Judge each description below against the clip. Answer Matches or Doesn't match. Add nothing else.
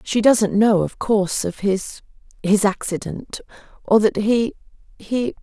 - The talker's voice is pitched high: Matches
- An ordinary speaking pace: Doesn't match